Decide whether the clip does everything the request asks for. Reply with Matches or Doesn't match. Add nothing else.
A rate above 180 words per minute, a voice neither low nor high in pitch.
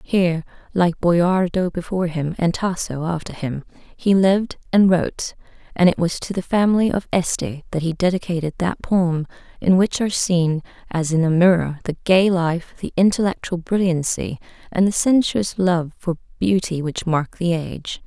Doesn't match